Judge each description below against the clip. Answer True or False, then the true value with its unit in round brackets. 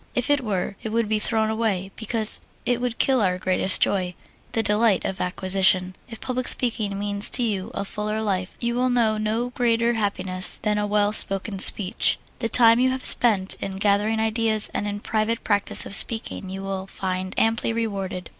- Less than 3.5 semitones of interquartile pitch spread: True (2.8 semitones)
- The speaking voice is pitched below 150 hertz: False (215 Hz)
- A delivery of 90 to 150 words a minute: False (190 wpm)